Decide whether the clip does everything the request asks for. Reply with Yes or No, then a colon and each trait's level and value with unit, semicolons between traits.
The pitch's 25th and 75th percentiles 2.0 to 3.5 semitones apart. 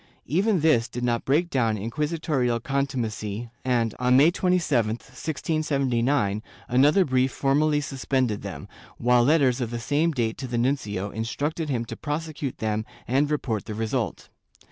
No: average, 4.2 semitones